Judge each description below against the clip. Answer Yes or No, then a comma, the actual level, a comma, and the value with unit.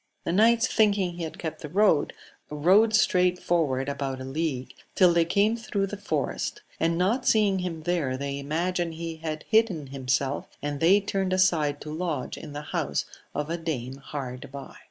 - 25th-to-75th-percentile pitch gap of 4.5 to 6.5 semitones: Yes, average, 4.8 semitones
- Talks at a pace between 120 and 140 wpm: No, average, 180 wpm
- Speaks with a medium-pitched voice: Yes, medium, 165 Hz